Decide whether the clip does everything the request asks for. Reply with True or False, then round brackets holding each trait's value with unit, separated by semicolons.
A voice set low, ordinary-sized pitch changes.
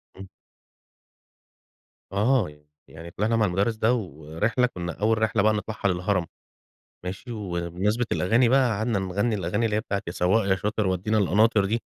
True (105 Hz; 3.5 semitones)